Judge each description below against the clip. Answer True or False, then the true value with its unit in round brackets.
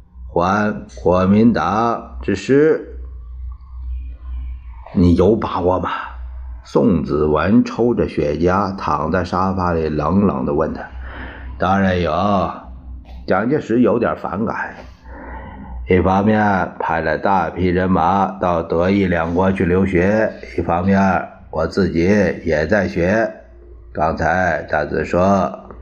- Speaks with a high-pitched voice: False (90 Hz)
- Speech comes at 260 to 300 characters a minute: False (160 characters per minute)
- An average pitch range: False (6.7 semitones)